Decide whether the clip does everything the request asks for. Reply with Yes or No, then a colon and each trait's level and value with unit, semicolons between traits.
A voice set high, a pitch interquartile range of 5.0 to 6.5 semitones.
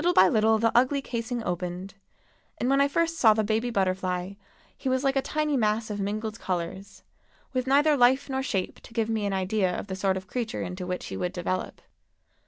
Yes: high, 220 Hz; wide, 5.4 semitones